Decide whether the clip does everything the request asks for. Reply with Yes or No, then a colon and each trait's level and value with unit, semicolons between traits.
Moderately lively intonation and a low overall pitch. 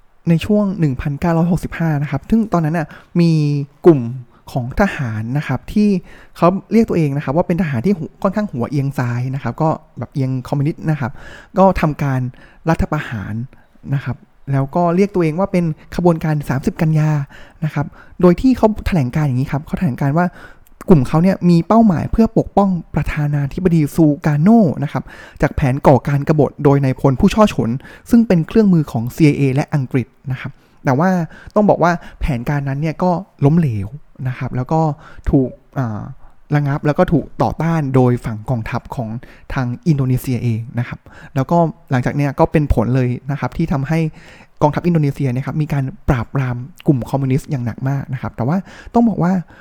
No: average, 4.6 semitones; medium, 150 Hz